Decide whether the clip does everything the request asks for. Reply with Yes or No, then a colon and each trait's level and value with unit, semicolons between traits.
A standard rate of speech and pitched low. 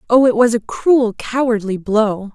No: average, 180 wpm; high, 230 Hz